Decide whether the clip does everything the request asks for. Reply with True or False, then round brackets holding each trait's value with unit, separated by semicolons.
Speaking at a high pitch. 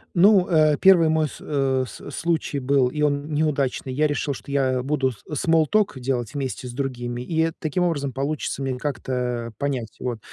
False (140 Hz)